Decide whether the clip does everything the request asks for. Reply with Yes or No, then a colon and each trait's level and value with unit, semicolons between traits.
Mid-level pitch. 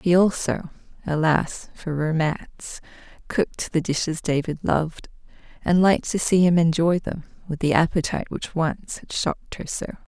Yes: medium, 165 Hz